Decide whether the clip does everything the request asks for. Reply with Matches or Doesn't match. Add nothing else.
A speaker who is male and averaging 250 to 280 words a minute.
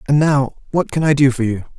Matches